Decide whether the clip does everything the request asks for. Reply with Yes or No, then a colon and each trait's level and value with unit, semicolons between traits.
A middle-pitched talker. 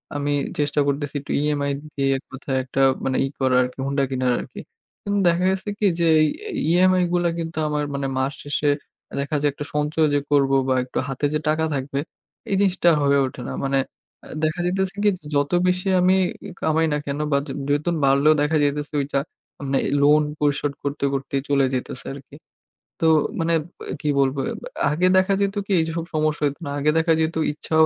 Yes: medium, 145 Hz